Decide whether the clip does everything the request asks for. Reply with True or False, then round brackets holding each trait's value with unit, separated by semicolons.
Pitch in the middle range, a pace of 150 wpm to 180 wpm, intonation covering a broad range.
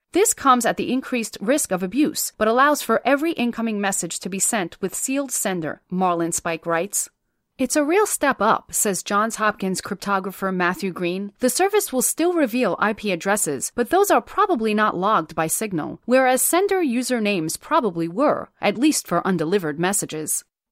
False (210 Hz; 170 wpm; 6.0 semitones)